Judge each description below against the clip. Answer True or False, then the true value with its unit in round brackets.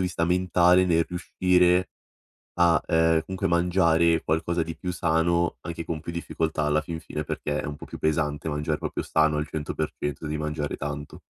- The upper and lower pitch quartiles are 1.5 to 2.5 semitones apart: True (2.0 semitones)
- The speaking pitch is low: True (80 Hz)